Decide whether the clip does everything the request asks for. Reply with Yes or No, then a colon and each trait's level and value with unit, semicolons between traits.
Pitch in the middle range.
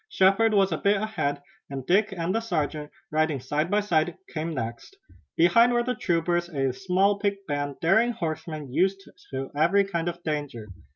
Yes: medium, 175 Hz